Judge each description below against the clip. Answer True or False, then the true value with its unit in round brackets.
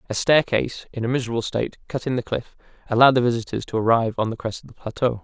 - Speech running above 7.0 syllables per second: True (7.5 syllables/s)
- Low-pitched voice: True (120 Hz)